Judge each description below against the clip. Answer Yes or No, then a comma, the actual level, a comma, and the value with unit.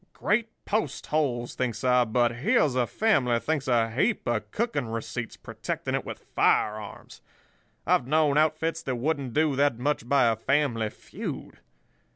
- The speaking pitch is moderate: No, low, 130 Hz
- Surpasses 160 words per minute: No, average, 155 wpm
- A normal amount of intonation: Yes, average, 4.5 semitones